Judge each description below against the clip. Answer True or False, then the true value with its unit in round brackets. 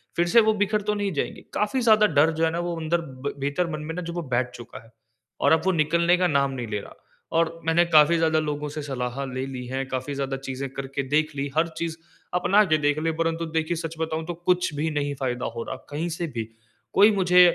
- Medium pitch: True (160 Hz)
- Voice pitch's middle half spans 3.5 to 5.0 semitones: True (3.9 semitones)